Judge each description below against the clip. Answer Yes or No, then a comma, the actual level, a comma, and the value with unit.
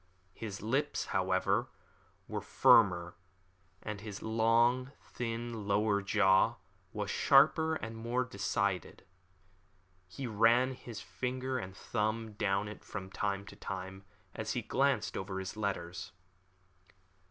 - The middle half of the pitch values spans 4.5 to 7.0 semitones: No, average, 3.3 semitones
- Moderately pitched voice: No, low, 105 Hz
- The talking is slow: Yes, slow, 120 wpm